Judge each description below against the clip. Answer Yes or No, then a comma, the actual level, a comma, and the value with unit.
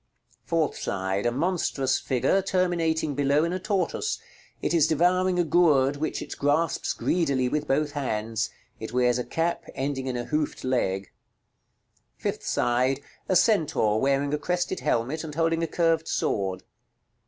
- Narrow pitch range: No, average, 4.8 semitones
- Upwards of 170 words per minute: No, average, 155 wpm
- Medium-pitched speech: Yes, medium, 145 Hz